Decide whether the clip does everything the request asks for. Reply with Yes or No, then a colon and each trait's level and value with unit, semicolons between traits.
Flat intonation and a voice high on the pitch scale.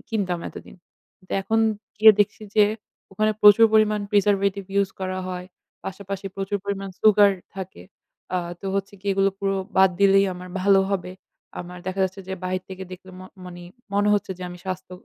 Yes: narrow, 1.5 semitones; high, 195 Hz